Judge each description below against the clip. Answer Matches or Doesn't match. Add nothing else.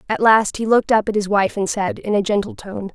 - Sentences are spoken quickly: Matches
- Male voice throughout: Doesn't match